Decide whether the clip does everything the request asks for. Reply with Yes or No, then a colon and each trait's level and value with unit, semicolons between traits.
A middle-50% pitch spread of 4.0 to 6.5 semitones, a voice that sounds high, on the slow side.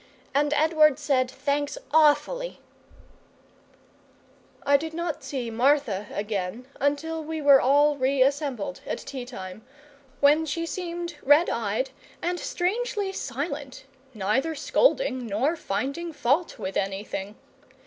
Yes: average, 4.3 semitones; very high, 285 Hz; slow, 120 wpm